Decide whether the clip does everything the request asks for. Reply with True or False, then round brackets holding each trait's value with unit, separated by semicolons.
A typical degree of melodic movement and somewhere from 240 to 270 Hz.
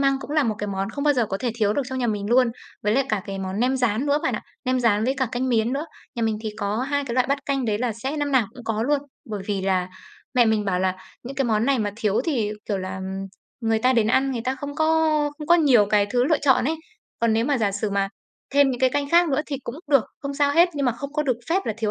True (4.6 semitones; 245 Hz)